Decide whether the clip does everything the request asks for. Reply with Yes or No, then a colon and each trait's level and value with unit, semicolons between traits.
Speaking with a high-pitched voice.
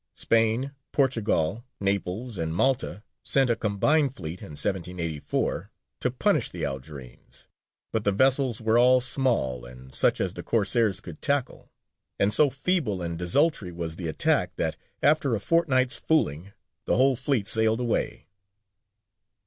No: low, 110 Hz